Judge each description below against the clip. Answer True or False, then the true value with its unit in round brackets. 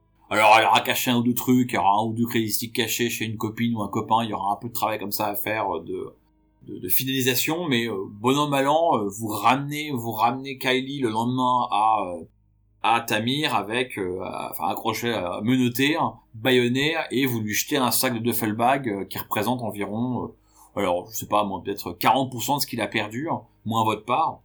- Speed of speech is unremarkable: True (205 wpm)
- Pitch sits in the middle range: False (115 Hz)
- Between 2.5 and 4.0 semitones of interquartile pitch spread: True (3.1 semitones)